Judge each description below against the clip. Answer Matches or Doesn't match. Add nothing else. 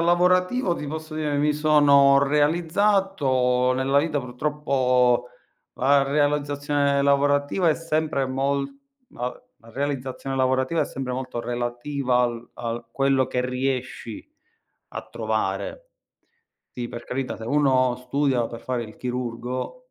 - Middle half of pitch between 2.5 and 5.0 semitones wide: Matches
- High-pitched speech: Doesn't match